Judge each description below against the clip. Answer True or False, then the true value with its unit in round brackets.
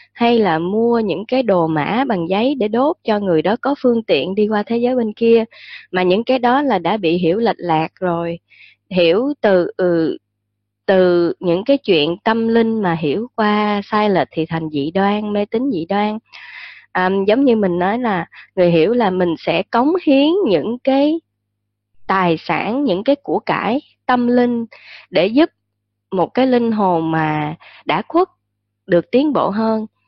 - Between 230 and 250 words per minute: False (185 wpm)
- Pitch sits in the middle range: False (205 Hz)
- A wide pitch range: True (5.9 semitones)